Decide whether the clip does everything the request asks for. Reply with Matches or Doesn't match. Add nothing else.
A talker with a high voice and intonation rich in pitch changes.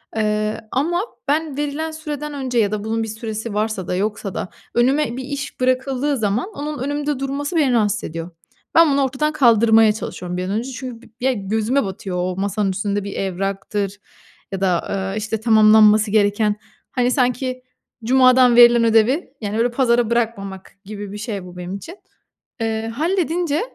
Doesn't match